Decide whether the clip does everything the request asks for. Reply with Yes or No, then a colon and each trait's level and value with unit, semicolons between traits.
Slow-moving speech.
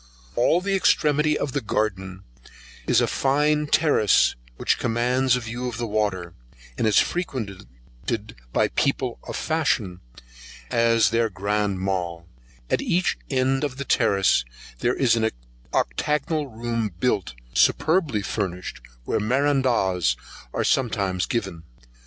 Yes: slow, 130 wpm